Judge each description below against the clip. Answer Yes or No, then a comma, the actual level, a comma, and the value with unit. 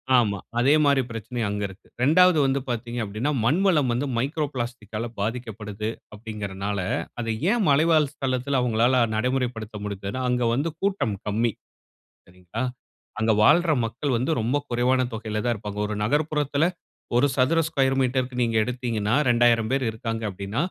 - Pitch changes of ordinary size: Yes, average, 3.8 semitones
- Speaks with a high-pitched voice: No, low, 120 Hz